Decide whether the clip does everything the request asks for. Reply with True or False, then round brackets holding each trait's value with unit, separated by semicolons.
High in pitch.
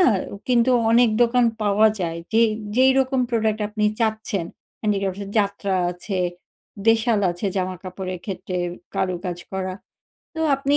True (210 Hz)